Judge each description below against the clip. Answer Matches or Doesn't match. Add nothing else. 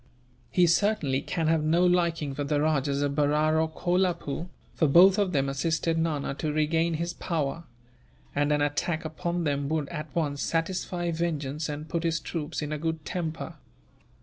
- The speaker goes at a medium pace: Matches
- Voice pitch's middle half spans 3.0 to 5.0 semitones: Doesn't match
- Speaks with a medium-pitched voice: Matches